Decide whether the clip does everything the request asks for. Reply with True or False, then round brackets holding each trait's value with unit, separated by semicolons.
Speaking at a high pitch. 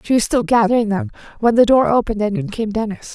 True (220 Hz)